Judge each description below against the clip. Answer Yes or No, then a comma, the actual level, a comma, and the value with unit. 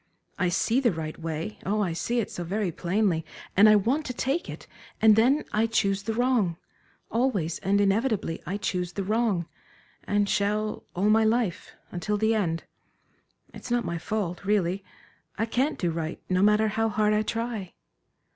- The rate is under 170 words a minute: No, average, 175 wpm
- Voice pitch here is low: No, high, 210 Hz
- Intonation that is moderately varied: Yes, average, 3.8 semitones